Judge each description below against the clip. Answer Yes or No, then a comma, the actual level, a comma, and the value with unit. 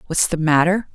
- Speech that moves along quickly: No, average, 190 wpm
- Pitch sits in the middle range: Yes, medium, 170 Hz